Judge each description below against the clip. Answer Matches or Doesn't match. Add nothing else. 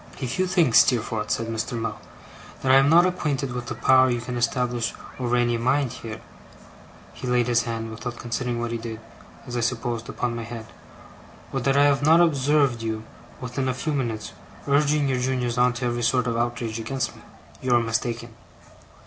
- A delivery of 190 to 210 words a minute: Matches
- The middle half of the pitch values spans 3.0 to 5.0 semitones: Doesn't match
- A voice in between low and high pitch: Doesn't match